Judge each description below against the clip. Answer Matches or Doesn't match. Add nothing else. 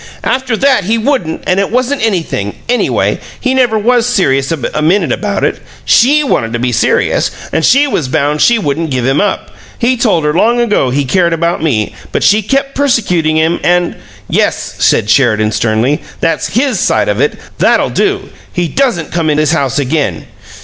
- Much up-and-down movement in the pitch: Matches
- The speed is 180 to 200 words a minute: Matches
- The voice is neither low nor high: Matches